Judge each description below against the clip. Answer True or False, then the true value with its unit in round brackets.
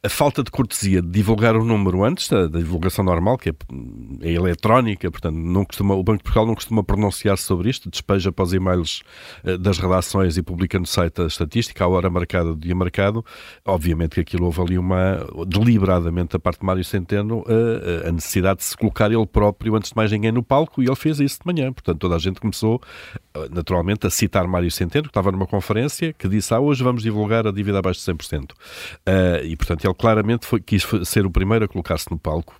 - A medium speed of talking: False (215 wpm)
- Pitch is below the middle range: True (95 Hz)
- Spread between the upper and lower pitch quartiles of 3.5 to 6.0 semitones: True (3.8 semitones)